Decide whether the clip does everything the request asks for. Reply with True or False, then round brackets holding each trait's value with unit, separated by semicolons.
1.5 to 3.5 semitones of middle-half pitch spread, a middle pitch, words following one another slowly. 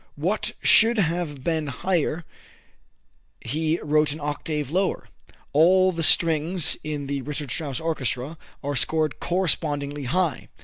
True (2.8 semitones; 155 Hz; 125 wpm)